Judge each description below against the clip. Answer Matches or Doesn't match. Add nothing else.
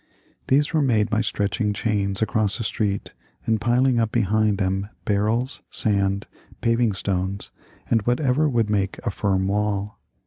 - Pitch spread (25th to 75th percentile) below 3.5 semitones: Matches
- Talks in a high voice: Doesn't match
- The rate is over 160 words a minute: Doesn't match